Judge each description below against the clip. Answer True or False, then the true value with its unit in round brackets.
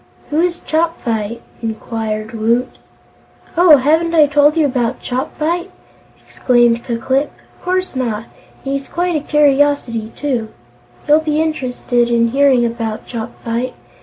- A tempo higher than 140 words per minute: False (135 wpm)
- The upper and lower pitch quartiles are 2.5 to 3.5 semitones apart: False (4.7 semitones)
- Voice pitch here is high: True (260 Hz)